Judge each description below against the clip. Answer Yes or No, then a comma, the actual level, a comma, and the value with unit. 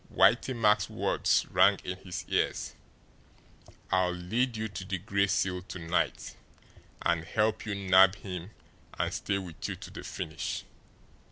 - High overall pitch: No, very low, 95 Hz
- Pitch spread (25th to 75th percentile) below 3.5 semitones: Yes, average, 2.7 semitones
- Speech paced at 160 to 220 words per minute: No, average, 150 wpm